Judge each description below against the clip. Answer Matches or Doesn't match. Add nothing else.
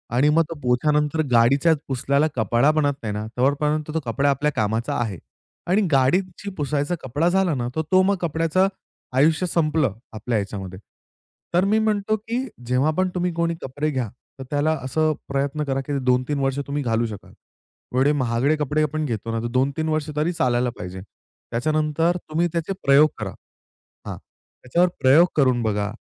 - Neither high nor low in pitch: Matches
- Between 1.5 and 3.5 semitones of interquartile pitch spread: Doesn't match